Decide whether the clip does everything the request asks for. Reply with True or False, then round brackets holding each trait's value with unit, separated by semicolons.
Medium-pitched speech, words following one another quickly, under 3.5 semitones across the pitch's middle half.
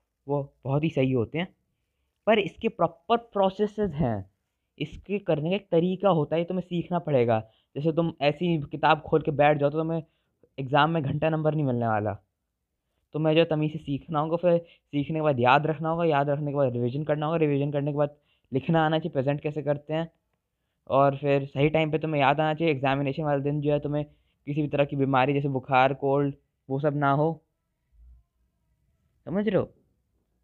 True (150 Hz; 200 wpm; 3.0 semitones)